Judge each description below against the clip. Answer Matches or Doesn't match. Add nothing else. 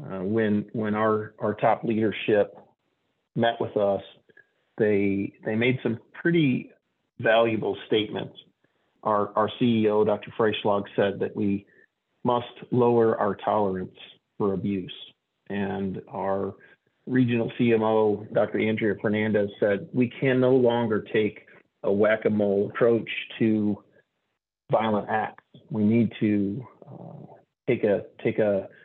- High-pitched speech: Doesn't match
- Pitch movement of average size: Doesn't match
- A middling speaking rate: Doesn't match